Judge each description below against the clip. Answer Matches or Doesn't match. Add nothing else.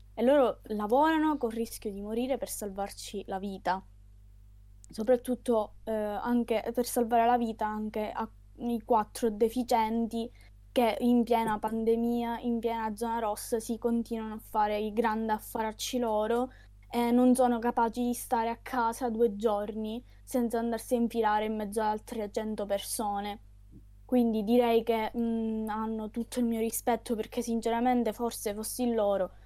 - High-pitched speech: Matches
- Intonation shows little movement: Matches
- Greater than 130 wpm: Matches